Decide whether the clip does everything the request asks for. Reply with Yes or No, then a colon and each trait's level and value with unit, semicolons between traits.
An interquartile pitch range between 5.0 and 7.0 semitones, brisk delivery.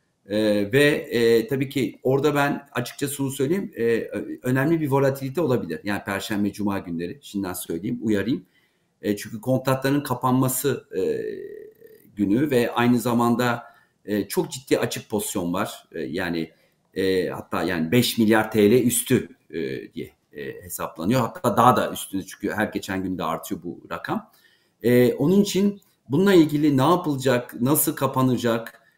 Yes: wide, 5.6 semitones; fast, 145 wpm